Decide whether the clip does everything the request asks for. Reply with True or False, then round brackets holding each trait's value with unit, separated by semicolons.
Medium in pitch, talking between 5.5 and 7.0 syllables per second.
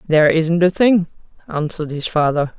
True (165 Hz; 5.6 syllables/s)